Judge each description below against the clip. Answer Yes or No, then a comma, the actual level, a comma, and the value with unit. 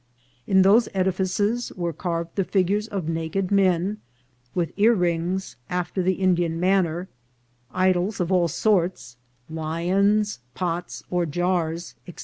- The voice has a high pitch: No, medium, 180 Hz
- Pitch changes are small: Yes, narrow, 2.3 semitones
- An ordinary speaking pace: No, slow, 125 wpm